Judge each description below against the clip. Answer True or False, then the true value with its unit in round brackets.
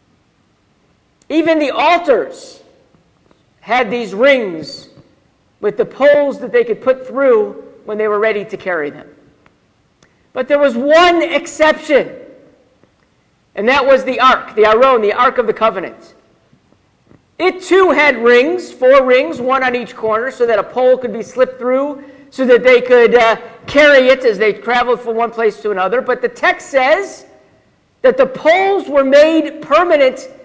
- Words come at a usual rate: True (160 wpm)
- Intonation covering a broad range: False (4.3 semitones)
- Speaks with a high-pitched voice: True (265 Hz)